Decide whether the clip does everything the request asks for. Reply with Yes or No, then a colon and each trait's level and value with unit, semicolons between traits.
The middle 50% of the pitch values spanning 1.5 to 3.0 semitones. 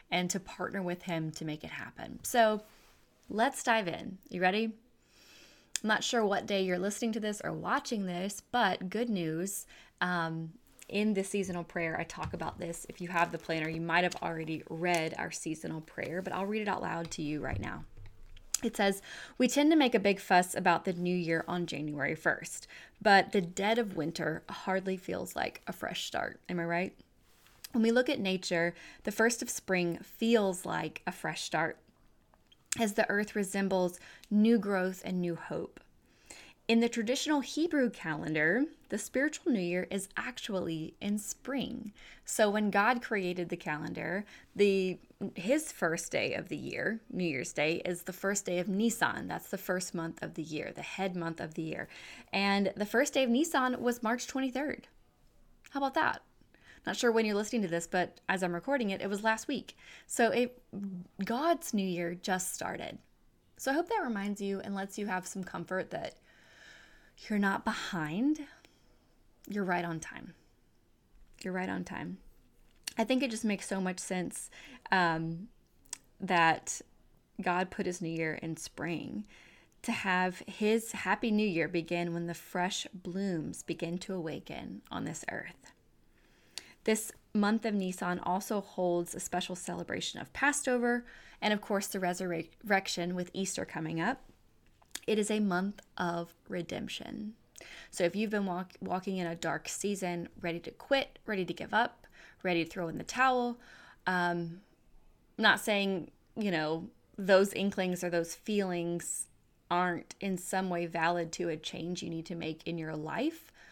No: average, 4.2 semitones